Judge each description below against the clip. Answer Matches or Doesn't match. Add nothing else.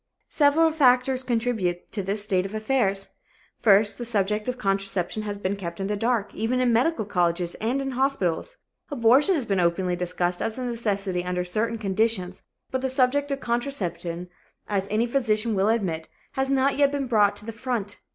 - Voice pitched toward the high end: Matches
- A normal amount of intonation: Matches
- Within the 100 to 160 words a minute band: Doesn't match